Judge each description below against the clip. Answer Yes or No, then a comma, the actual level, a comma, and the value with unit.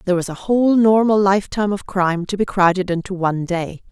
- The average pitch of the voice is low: No, high, 190 Hz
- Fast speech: Yes, fast, 215 wpm